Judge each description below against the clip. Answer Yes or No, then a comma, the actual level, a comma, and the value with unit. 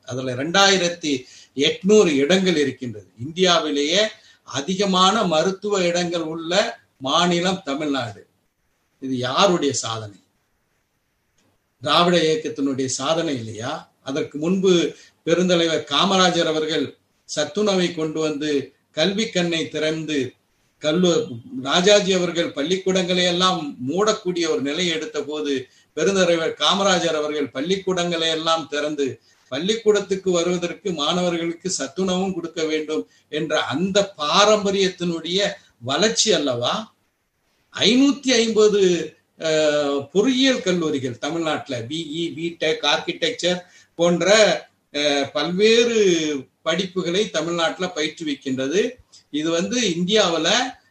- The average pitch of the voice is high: No, medium, 165 Hz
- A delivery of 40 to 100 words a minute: Yes, average, 85 wpm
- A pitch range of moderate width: Yes, average, 4.0 semitones